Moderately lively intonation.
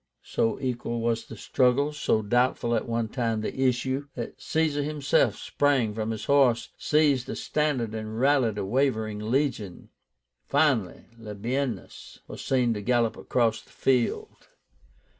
Yes: average, 3.6 semitones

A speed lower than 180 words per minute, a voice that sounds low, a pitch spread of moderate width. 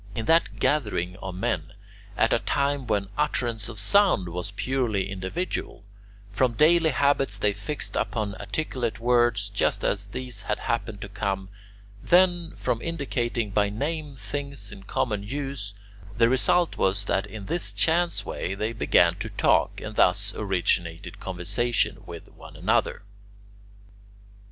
No: average, 140 wpm; low, 110 Hz; wide, 5.8 semitones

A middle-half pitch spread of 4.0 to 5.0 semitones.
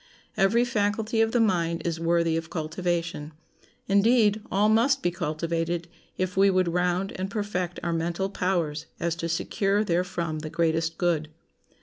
No: average, 3.2 semitones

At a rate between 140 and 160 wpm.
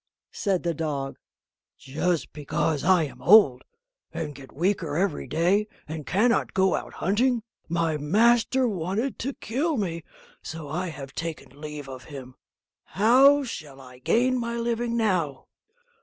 Yes: average, 145 wpm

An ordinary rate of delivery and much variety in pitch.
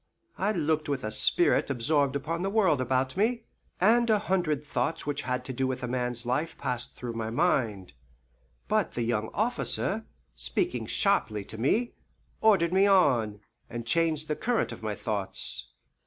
Yes: average, 165 wpm; wide, 7.6 semitones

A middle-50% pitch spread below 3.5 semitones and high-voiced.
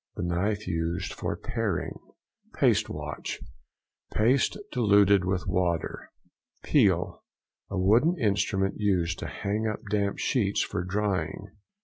No: average, 2.9 semitones; low, 100 Hz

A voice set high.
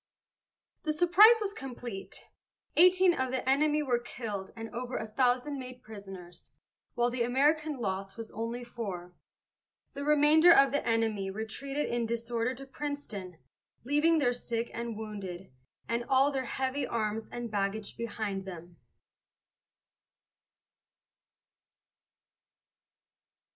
Yes: high, 240 Hz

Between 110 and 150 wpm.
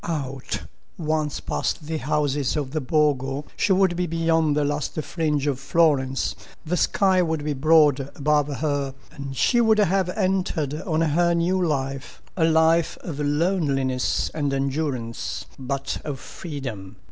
Yes: average, 145 wpm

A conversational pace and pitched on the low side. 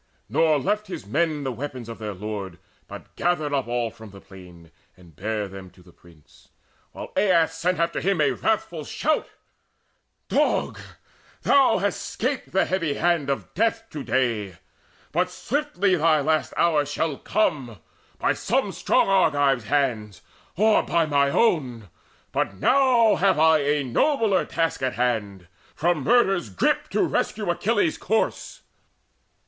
No: average, 150 wpm; medium, 150 Hz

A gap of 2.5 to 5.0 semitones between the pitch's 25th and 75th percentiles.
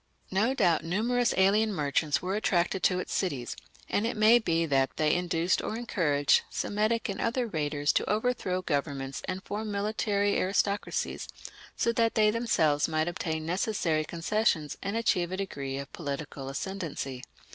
No: wide, 5.5 semitones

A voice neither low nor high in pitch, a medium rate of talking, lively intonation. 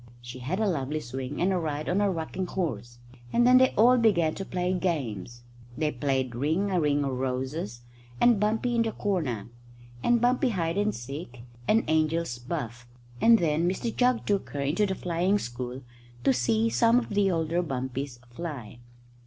Yes: medium, 160 Hz; average, 180 wpm; wide, 7.4 semitones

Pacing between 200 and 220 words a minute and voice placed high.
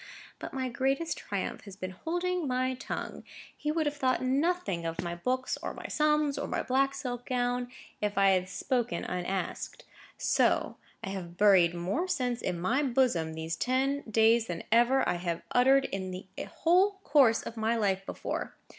No: average, 175 wpm; high, 245 Hz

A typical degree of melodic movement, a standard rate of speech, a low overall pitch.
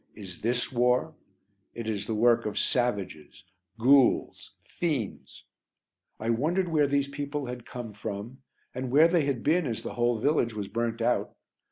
Yes: average, 4.1 semitones; average, 160 wpm; low, 120 Hz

